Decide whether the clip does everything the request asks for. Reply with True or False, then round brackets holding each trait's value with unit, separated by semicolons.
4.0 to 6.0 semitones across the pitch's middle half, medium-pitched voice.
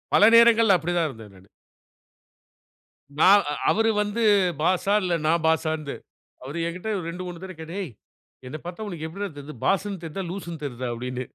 True (4.3 semitones; 170 Hz)